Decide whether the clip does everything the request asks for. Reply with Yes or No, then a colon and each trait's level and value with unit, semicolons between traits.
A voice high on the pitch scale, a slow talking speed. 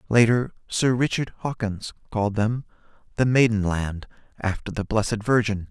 No: low, 110 Hz; slow, 125 wpm